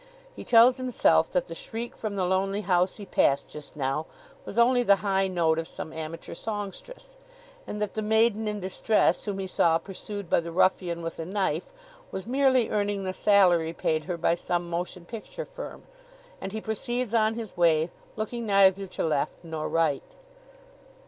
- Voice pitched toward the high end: Yes, high, 195 Hz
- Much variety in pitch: No, average, 4.5 semitones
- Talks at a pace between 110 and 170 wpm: No, average, 180 wpm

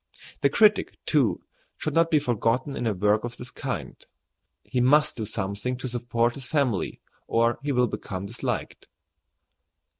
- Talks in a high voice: No, low, 120 Hz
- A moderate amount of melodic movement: Yes, average, 3.4 semitones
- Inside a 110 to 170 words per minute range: Yes, average, 155 wpm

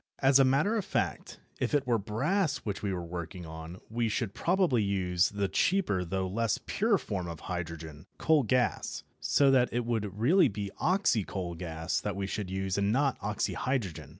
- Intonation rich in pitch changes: Yes, wide, 6.5 semitones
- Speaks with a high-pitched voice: No, low, 105 Hz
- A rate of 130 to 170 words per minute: No, average, 180 wpm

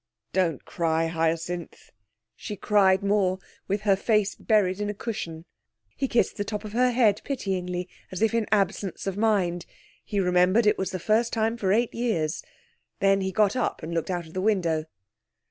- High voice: Yes, high, 195 Hz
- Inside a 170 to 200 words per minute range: Yes, average, 180 wpm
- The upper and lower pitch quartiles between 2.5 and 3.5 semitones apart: Yes, average, 3.2 semitones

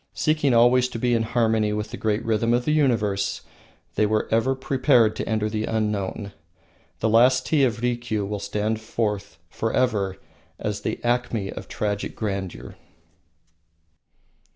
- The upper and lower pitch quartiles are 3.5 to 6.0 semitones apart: No, narrow, 2.6 semitones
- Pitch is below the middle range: Yes, low, 110 Hz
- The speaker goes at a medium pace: Yes, average, 150 wpm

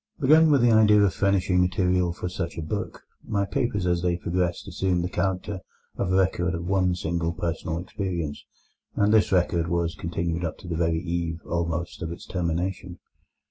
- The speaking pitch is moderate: No, very low, 90 Hz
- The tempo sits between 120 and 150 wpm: No, average, 180 wpm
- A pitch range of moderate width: No, narrow, 2.0 semitones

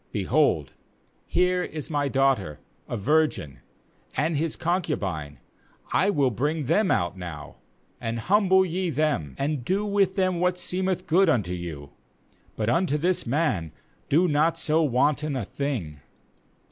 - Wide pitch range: Yes, wide, 8.8 semitones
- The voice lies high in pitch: No, medium, 150 Hz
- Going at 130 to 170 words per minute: Yes, average, 140 wpm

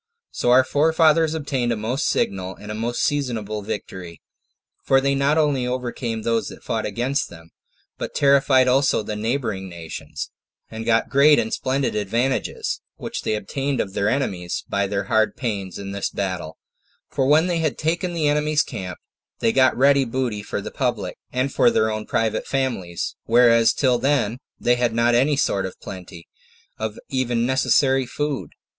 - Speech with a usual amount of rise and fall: Yes, average, 4.7 semitones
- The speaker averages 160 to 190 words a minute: Yes, average, 170 wpm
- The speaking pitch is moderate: No, low, 120 Hz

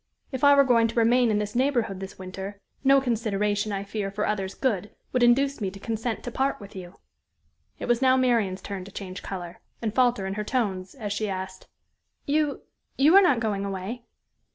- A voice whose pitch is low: No, high, 215 Hz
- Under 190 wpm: No, average, 200 wpm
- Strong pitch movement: No, average, 4.2 semitones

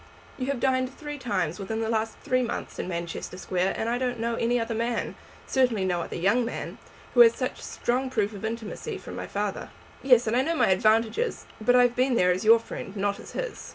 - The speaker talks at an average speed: No, fast, 230 wpm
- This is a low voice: No, high, 230 Hz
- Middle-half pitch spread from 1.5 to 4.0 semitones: Yes, average, 3.7 semitones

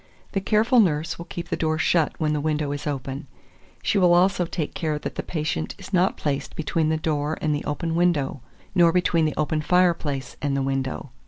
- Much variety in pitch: No, average, 3.0 semitones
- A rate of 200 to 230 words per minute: Yes, fast, 205 wpm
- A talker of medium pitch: Yes, medium, 155 Hz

